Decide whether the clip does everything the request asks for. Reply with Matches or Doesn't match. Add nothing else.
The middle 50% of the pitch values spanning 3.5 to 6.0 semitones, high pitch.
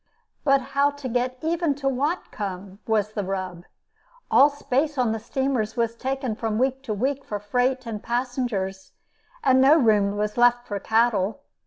Matches